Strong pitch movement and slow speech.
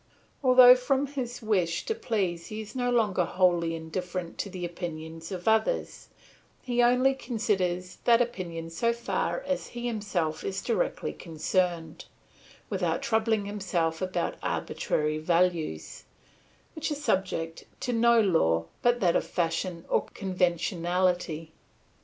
Yes: wide, 5.7 semitones; slow, 130 wpm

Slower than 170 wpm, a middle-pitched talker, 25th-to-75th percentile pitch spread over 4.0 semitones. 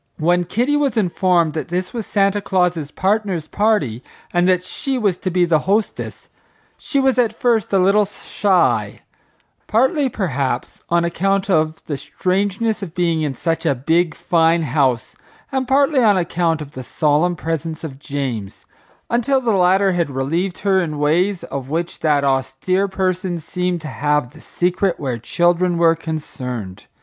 Yes: average, 160 wpm; medium, 175 Hz; average, 4.4 semitones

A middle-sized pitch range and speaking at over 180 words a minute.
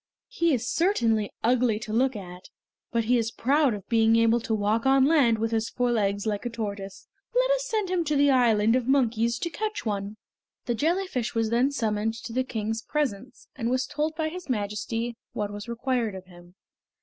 Yes: average, 3.8 semitones; average, 200 wpm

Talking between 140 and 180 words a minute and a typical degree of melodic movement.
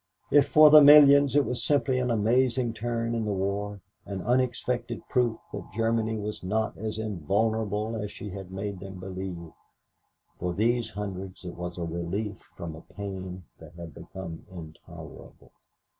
Yes: average, 160 wpm; average, 4.0 semitones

